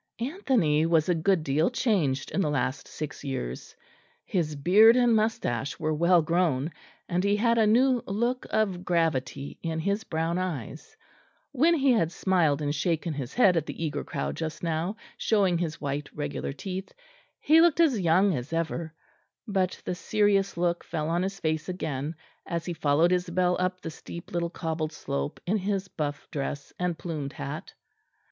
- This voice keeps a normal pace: Yes, average, 170 wpm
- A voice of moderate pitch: Yes, medium, 170 Hz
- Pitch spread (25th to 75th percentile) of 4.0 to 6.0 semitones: Yes, average, 4.4 semitones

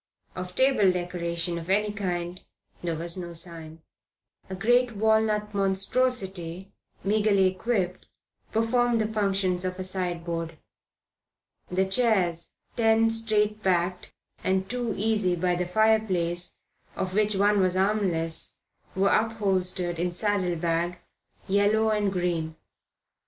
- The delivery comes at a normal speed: No, slow, 115 wpm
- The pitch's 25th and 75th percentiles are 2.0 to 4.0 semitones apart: Yes, average, 3.4 semitones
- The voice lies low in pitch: No, high, 190 Hz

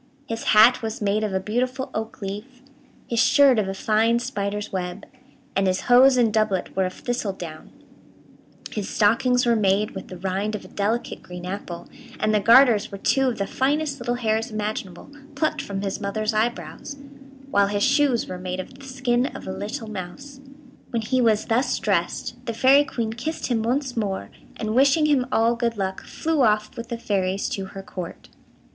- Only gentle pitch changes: No, average, 4.0 semitones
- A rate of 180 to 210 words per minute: Yes, average, 190 wpm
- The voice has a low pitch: No, high, 220 Hz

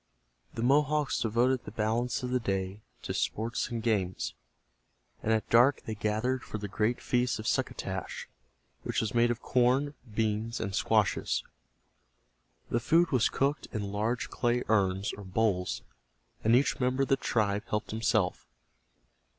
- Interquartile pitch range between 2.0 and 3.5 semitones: Yes, average, 2.9 semitones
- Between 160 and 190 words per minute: No, average, 150 wpm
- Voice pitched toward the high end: No, low, 115 Hz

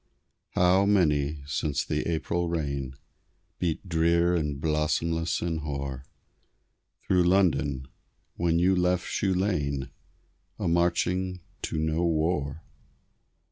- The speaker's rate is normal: No, slow, 105 wpm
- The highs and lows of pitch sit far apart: No, average, 3.1 semitones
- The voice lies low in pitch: Yes, very low, 80 Hz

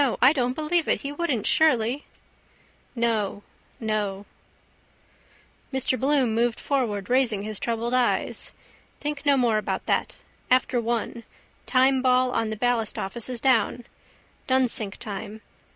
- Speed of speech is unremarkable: No, slow, 120 wpm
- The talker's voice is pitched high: Yes, high, 245 Hz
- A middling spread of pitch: Yes, average, 3.2 semitones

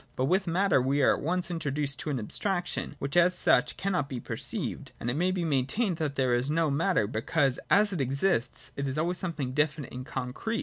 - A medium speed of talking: No, fast, 215 wpm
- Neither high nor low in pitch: Yes, medium, 150 Hz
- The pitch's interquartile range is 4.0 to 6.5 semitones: Yes, average, 5.1 semitones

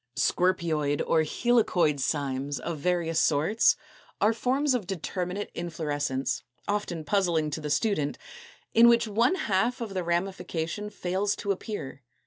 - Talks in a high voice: No, medium, 180 Hz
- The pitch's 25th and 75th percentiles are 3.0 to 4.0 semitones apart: No, average, 5.1 semitones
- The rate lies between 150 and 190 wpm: No, slow, 135 wpm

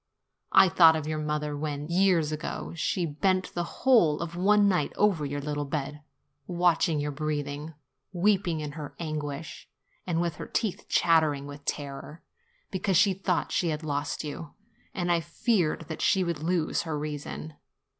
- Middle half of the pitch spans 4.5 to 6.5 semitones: No, average, 3.0 semitones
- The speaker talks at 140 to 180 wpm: Yes, average, 170 wpm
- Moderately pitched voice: Yes, medium, 160 Hz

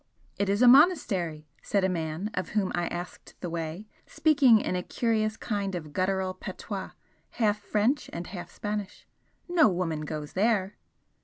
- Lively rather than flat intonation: No, average, 3.7 semitones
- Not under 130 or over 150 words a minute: No, average, 160 wpm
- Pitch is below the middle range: No, high, 195 Hz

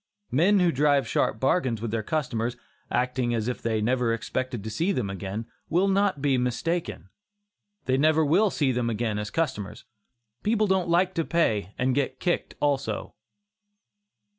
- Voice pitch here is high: No, low, 130 Hz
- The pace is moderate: Yes, average, 165 wpm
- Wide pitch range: Yes, wide, 6.4 semitones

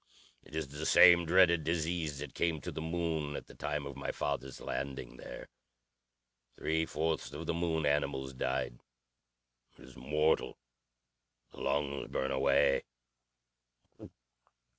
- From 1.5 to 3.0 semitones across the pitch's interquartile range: Yes, average, 2.7 semitones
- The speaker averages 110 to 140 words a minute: Yes, slow, 135 wpm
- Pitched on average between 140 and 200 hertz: No, very low, 75 Hz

